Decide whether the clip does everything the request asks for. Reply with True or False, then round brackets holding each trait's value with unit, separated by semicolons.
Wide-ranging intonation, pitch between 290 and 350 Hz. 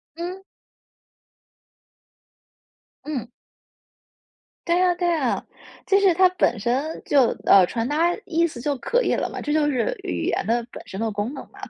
True (6.5 semitones; 295 Hz)